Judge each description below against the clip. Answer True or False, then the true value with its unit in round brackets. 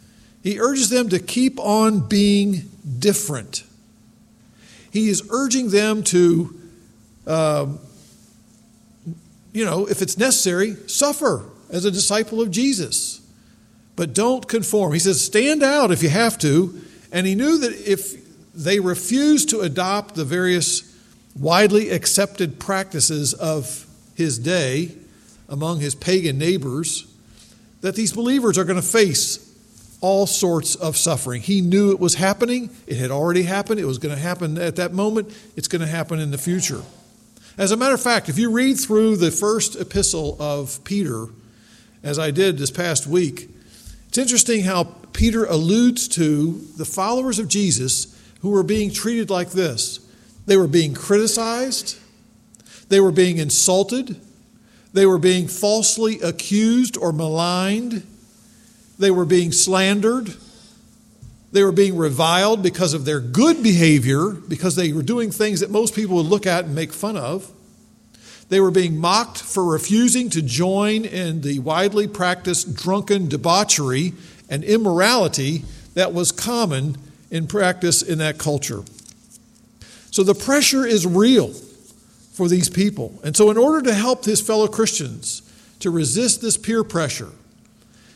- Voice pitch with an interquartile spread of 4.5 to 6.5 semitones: True (4.8 semitones)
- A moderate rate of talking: True (150 wpm)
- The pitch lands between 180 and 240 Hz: True (190 Hz)